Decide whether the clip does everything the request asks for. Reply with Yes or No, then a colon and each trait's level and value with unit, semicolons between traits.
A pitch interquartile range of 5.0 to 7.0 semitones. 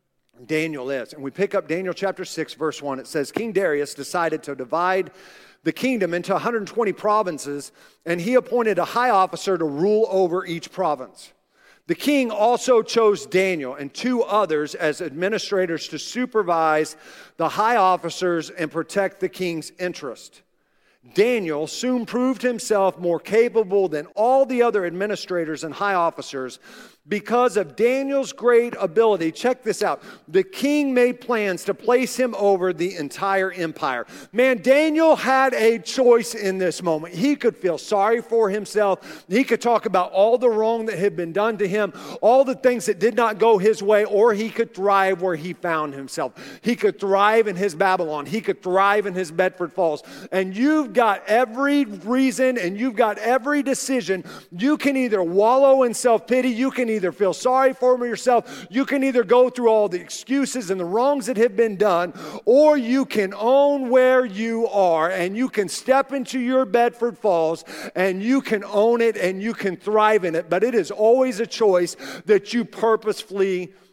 Yes: average, 5.3 semitones